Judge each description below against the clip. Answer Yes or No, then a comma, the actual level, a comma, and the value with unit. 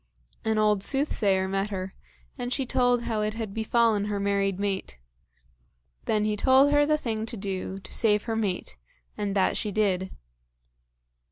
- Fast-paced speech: No, average, 165 wpm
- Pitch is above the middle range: Yes, high, 210 Hz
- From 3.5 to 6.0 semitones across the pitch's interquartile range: No, average, 2.9 semitones